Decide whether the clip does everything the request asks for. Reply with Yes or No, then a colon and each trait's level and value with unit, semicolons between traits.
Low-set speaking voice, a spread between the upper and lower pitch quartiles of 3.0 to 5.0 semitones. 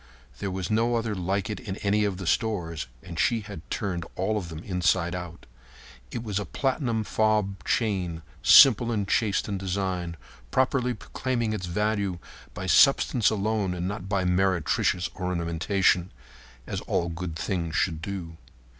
Yes: very low, 95 Hz; average, 3.6 semitones